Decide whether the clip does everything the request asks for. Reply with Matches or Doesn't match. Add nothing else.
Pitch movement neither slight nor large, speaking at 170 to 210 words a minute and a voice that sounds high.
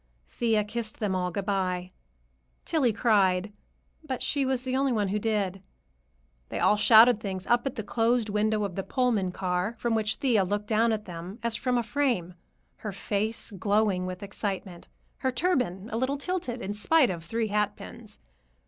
Matches